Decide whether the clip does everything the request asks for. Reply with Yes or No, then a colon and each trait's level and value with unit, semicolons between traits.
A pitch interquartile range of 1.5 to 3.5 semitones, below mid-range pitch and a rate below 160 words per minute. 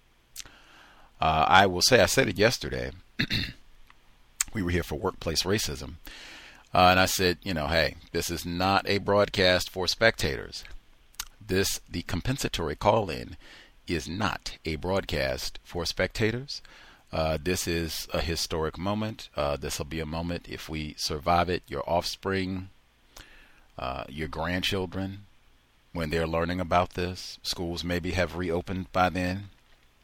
Yes: average, 3.0 semitones; very low, 85 Hz; average, 140 wpm